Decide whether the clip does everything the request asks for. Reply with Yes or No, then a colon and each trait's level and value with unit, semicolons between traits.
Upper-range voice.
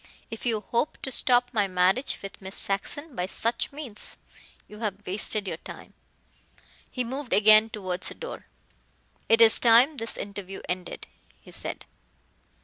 Yes: high, 220 Hz